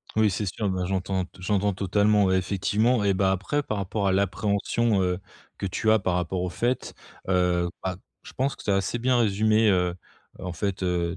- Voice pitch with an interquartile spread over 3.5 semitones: No, average, 2.7 semitones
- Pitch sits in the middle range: No, very low, 95 Hz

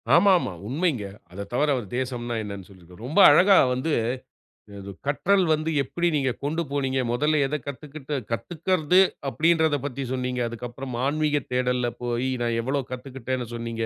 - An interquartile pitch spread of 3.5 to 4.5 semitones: Yes, average, 4.2 semitones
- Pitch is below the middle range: Yes, low, 130 Hz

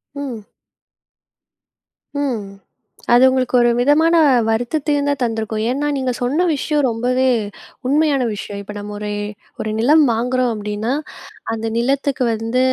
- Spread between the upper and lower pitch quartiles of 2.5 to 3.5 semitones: No, average, 4.1 semitones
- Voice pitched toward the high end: Yes, very high, 250 Hz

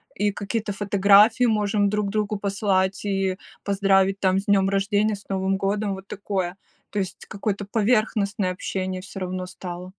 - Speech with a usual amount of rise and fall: No, narrow, 1.4 semitones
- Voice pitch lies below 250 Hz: Yes, high, 200 Hz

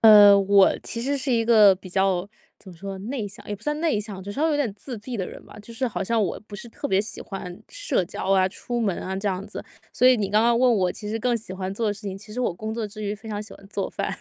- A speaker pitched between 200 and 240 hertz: Yes, high, 210 Hz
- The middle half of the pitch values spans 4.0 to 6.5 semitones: No, average, 3.1 semitones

